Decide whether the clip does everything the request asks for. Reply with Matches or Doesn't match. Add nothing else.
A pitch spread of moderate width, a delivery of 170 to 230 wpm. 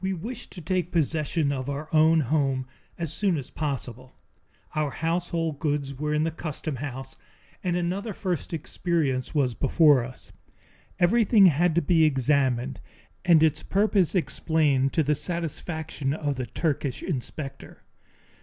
Doesn't match